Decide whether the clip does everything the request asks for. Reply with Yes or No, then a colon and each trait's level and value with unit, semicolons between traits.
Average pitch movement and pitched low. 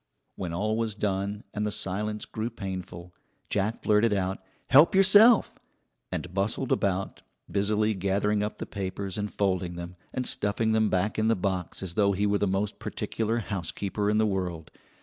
No: narrow, 2.3 semitones; low, 100 Hz